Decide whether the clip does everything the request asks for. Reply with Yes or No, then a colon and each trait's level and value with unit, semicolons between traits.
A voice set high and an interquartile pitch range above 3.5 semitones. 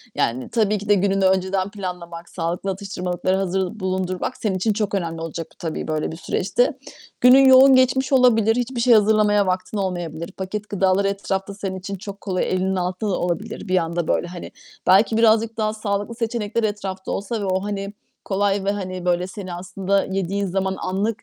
No: high, 195 Hz; narrow, 2.5 semitones